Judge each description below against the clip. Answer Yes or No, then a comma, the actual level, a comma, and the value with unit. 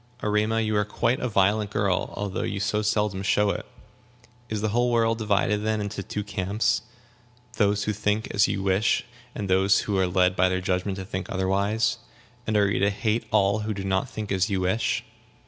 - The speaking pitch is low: Yes, low, 105 Hz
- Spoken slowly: No, average, 200 wpm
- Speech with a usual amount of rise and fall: No, narrow, 1.9 semitones